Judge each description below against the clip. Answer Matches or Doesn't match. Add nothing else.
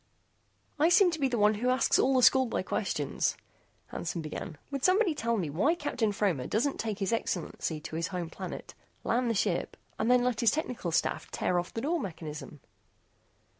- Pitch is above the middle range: Matches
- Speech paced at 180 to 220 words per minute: Matches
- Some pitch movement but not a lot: Doesn't match